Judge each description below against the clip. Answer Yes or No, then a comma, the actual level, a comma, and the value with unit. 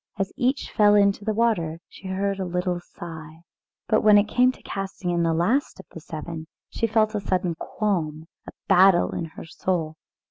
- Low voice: No, high, 190 Hz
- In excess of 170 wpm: Yes, average, 200 wpm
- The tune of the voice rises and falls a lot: No, average, 3.9 semitones